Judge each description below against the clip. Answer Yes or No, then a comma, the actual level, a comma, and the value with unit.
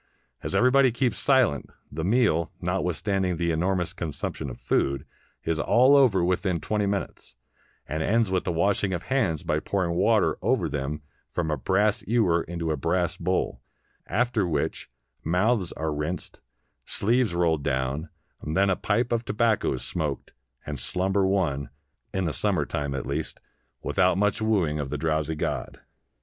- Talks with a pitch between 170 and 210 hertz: No, very low, 90 Hz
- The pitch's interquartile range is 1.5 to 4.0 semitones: No, average, 4.6 semitones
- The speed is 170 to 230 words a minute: No, average, 155 wpm